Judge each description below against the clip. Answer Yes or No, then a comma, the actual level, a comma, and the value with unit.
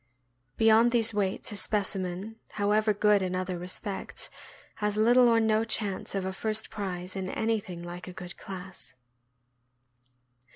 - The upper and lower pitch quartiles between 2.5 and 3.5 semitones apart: Yes, average, 2.9 semitones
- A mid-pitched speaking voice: No, high, 205 Hz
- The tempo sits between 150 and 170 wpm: No, average, 140 wpm